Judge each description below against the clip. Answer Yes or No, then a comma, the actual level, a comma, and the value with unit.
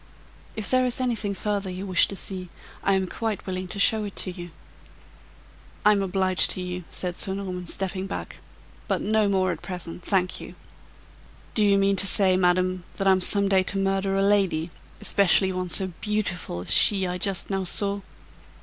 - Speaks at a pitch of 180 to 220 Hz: Yes, high, 190 Hz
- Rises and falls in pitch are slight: Yes, narrow, 1.5 semitones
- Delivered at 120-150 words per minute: No, average, 185 wpm